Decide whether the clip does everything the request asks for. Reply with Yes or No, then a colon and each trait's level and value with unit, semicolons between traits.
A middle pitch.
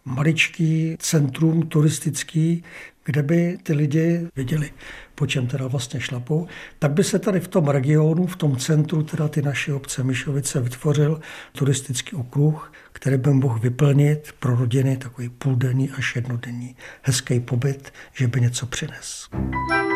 Yes: medium, 145 Hz